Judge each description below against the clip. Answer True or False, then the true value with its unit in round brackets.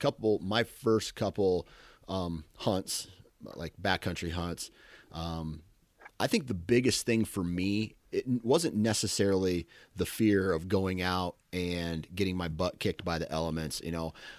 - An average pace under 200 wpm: True (145 wpm)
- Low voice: True (90 Hz)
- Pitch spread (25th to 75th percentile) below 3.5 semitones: False (4.0 semitones)